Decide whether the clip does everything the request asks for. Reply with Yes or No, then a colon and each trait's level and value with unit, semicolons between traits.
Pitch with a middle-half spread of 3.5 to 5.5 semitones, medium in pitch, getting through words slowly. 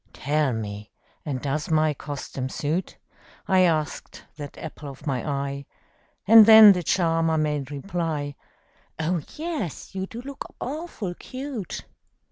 Yes: average, 5.0 semitones; medium, 155 Hz; slow, 130 wpm